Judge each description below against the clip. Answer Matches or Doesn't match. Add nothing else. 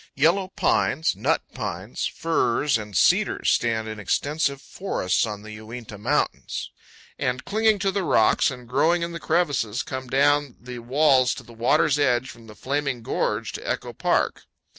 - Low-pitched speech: Matches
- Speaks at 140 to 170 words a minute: Matches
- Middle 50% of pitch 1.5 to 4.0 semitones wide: Doesn't match